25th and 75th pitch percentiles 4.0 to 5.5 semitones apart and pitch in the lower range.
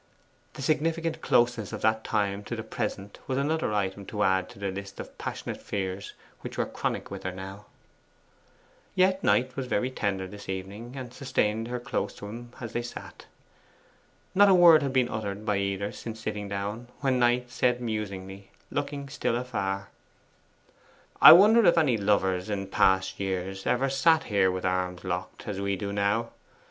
Yes: average, 4.4 semitones; low, 105 Hz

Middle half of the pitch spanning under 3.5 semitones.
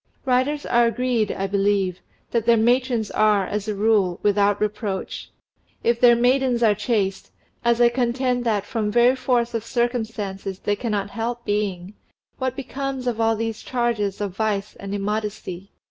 Yes: average, 2.8 semitones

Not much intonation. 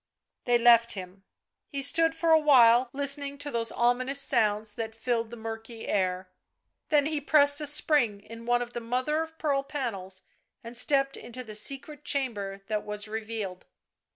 No: average, 4.4 semitones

